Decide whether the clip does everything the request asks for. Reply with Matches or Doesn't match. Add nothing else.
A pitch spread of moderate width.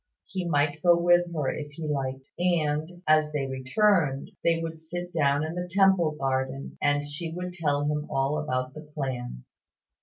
Matches